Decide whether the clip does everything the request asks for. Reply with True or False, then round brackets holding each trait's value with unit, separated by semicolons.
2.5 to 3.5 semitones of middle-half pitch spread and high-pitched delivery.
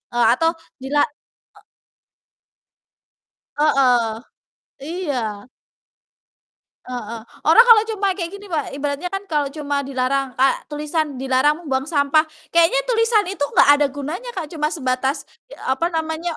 False (4.2 semitones; 295 Hz)